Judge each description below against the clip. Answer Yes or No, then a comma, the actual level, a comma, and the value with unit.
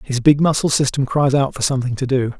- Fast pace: Yes, fast, 250 wpm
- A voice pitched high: No, low, 135 Hz